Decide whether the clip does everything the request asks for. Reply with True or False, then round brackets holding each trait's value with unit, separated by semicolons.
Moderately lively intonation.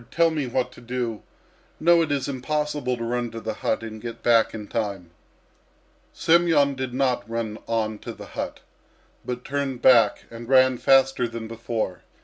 True (3.0 semitones)